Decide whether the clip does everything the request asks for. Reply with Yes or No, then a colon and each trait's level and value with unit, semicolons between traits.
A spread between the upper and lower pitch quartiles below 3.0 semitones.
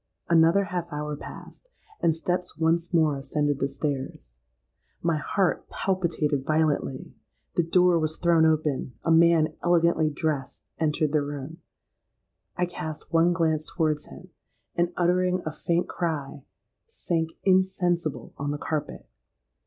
Yes: narrow, 2.6 semitones